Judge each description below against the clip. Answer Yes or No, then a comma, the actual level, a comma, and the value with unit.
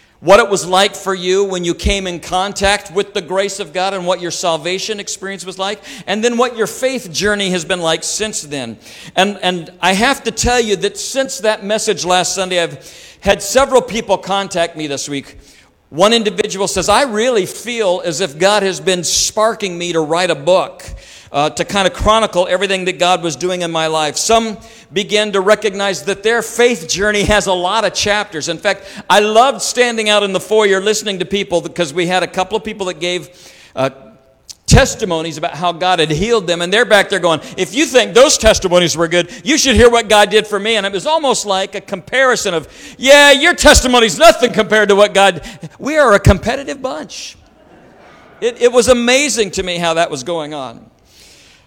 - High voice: Yes, high, 195 Hz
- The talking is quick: Yes, fast, 210 wpm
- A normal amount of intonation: Yes, average, 3.4 semitones